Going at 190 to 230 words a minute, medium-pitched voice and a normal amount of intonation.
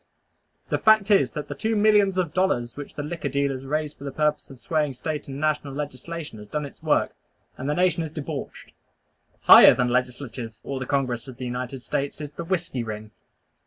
Yes: average, 200 wpm; medium, 145 Hz; average, 4.0 semitones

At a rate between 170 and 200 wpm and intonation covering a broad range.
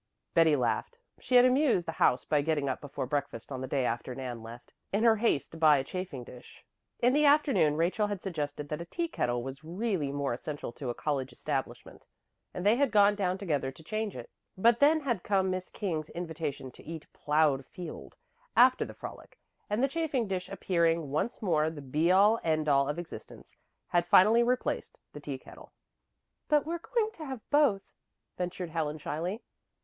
Yes: average, 190 wpm; wide, 7.1 semitones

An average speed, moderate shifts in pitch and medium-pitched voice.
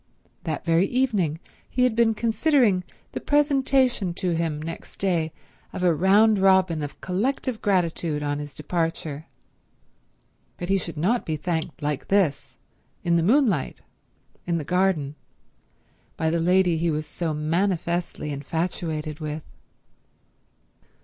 No: slow, 130 wpm; average, 4.0 semitones; medium, 170 Hz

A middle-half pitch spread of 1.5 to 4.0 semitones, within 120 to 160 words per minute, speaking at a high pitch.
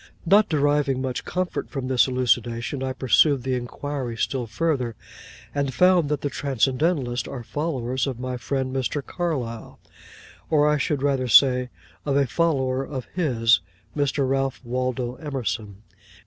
No: narrow, 2.6 semitones; average, 145 wpm; low, 130 Hz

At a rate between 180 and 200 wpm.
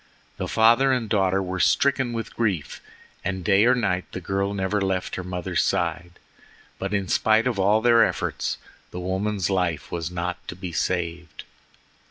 No: average, 170 wpm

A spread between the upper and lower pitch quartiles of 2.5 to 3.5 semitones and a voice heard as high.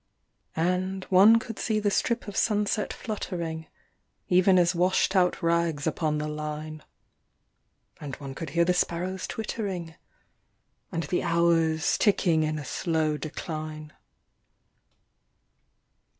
No: average, 3.2 semitones; medium, 170 Hz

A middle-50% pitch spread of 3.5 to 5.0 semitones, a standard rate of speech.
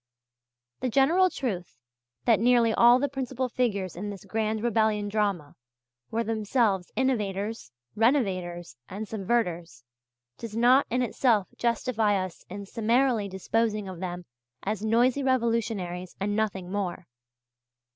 No: average, 3.8 semitones; slow, 125 wpm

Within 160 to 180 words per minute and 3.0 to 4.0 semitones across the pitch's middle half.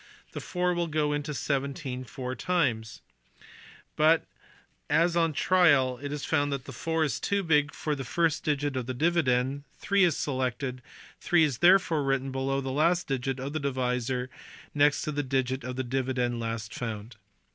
Yes: average, 175 wpm; average, 3.5 semitones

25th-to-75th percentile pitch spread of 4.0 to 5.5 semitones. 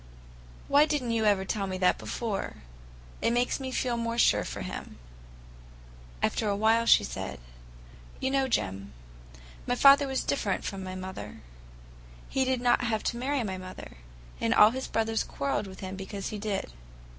Yes: average, 4.5 semitones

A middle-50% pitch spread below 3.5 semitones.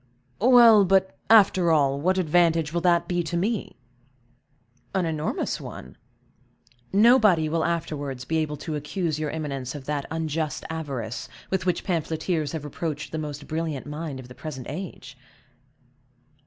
Yes: average, 3.1 semitones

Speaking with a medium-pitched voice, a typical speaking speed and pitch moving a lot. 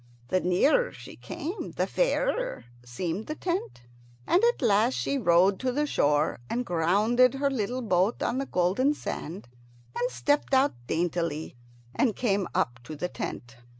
No: high, 215 Hz; average, 155 wpm; wide, 7.7 semitones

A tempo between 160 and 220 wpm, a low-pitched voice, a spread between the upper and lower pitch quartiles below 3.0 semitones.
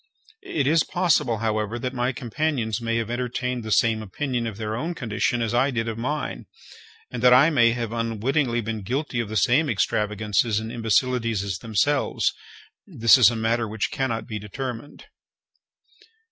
Yes: average, 165 wpm; low, 115 Hz; narrow, 2.5 semitones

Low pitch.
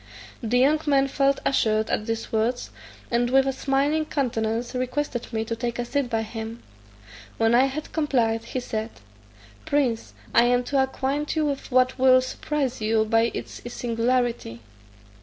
No: high, 245 Hz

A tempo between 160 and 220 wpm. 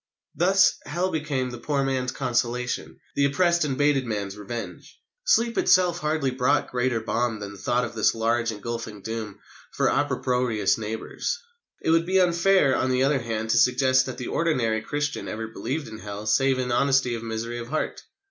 Yes: average, 175 wpm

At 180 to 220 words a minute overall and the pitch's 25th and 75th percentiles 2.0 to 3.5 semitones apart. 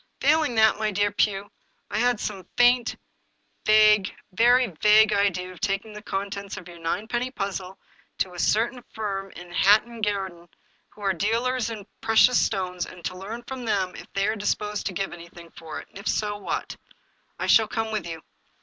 Yes: average, 190 wpm; average, 2.7 semitones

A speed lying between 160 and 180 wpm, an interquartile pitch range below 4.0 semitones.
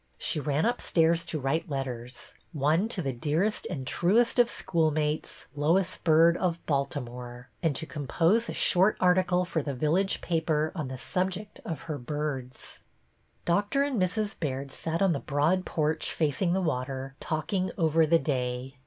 No: average, 165 wpm; average, 4.5 semitones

